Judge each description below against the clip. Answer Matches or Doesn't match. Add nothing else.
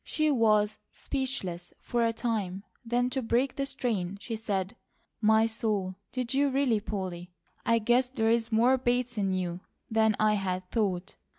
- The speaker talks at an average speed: Matches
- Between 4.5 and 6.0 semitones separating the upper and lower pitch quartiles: Doesn't match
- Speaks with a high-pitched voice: Matches